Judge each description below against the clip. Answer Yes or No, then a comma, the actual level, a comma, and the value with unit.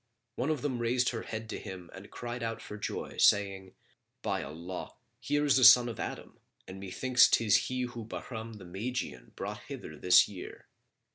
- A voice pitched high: No, low, 115 Hz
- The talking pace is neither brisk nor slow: Yes, average, 185 wpm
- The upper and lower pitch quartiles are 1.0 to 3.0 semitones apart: No, average, 4.5 semitones